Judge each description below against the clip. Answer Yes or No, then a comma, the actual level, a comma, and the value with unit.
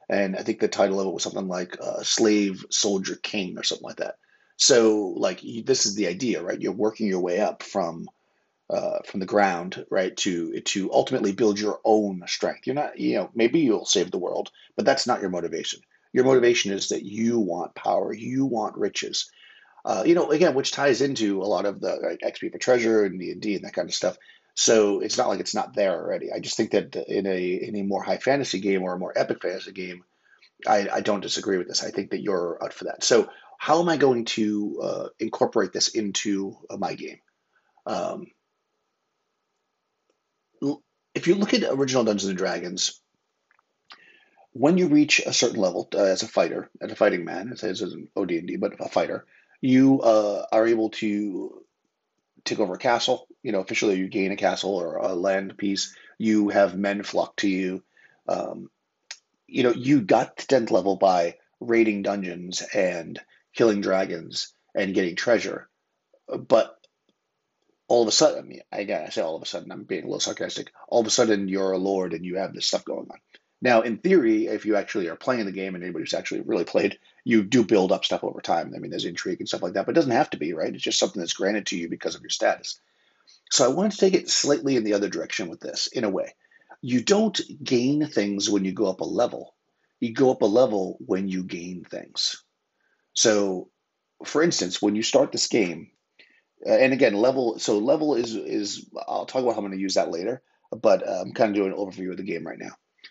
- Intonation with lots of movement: Yes, wide, 5.8 semitones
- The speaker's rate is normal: No, fast, 215 wpm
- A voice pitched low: Yes, low, 105 Hz